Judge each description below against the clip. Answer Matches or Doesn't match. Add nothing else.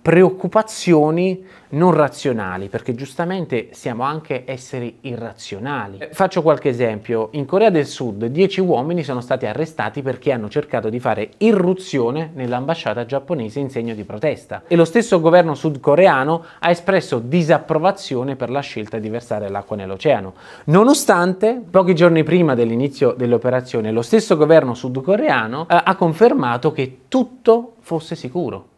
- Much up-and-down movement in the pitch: Matches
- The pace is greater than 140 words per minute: Doesn't match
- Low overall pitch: Doesn't match